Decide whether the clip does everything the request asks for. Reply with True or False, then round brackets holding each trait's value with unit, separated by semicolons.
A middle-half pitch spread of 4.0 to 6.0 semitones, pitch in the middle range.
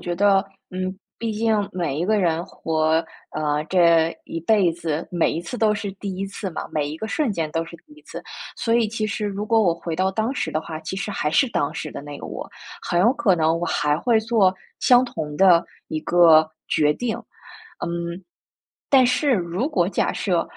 True (4.8 semitones; 180 Hz)